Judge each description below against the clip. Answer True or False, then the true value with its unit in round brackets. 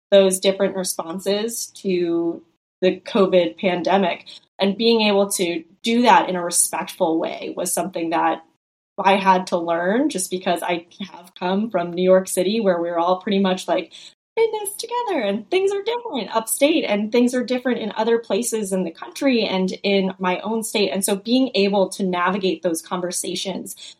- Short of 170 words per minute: False (175 wpm)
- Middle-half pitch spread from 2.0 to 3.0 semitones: False (3.7 semitones)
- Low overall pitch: False (195 Hz)